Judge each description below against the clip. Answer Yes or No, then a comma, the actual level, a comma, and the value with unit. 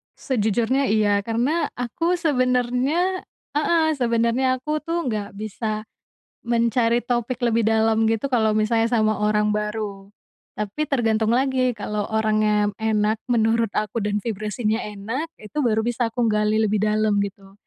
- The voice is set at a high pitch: Yes, high, 225 Hz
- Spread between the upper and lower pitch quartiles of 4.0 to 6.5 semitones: No, average, 2.8 semitones